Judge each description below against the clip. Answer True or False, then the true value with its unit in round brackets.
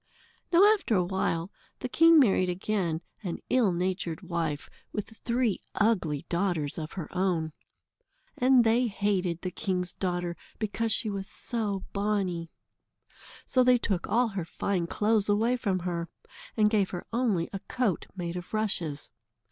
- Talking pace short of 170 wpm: True (150 wpm)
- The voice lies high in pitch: True (195 Hz)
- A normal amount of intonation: True (4.2 semitones)